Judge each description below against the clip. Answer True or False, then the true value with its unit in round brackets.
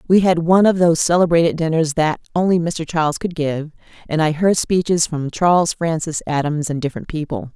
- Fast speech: False (190 wpm)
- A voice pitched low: False (165 Hz)